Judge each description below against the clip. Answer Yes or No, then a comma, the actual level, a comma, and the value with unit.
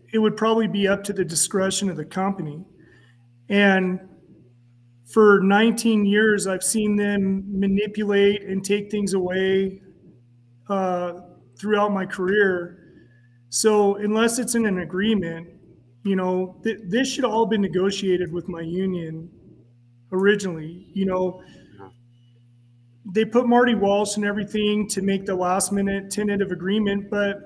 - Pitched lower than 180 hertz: No, high, 195 Hz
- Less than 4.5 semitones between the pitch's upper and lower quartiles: Yes, average, 2.9 semitones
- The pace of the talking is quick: No, slow, 135 wpm